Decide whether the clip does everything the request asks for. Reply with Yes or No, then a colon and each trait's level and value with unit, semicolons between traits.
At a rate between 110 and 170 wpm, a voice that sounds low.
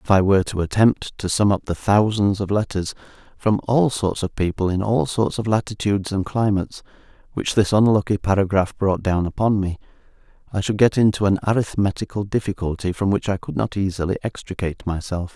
No: average, 185 wpm; low, 100 Hz